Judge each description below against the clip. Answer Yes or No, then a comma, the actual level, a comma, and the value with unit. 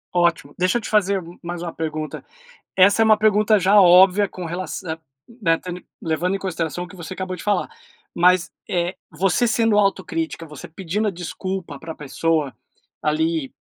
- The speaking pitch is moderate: Yes, medium, 180 Hz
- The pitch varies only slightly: No, average, 3.1 semitones